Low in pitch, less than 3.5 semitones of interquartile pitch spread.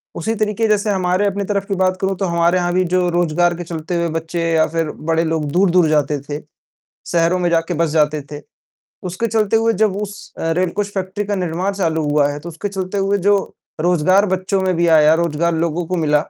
No: medium, 175 Hz; average, 3.0 semitones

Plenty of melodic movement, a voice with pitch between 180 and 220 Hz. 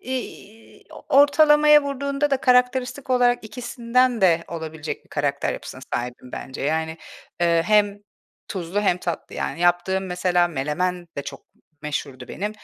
Yes: wide, 7.2 semitones; high, 190 Hz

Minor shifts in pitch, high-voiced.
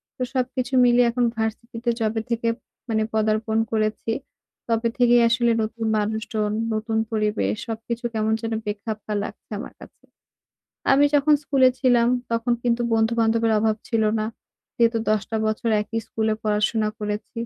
Yes: narrow, 1.6 semitones; high, 225 Hz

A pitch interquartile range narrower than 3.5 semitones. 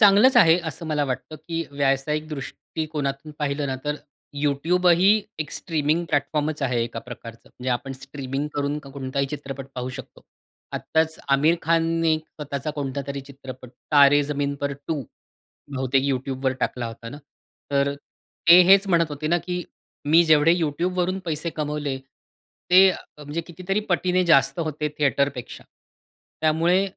Yes: average, 3.1 semitones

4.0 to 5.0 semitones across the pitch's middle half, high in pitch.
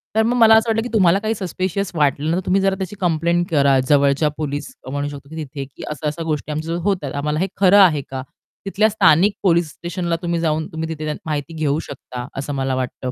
No: average, 4.7 semitones; medium, 160 Hz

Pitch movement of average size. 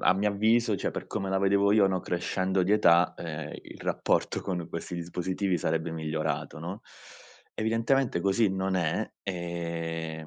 Yes: average, 3.2 semitones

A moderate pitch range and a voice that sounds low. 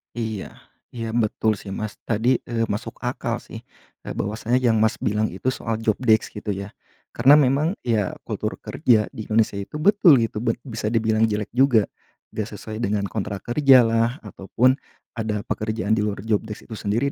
No: narrow, 2.3 semitones; low, 110 Hz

